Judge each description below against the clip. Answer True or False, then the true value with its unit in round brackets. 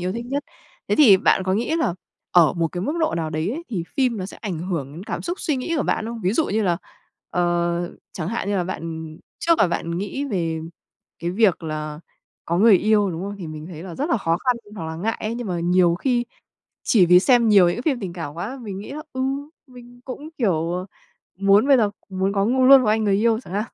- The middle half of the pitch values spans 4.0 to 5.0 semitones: False (5.4 semitones)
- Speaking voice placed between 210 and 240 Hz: False (195 Hz)